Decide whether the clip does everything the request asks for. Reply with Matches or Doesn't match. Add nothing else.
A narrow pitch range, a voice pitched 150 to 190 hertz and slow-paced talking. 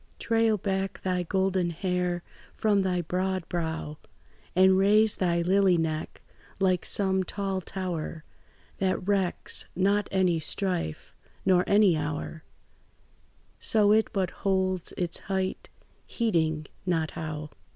Matches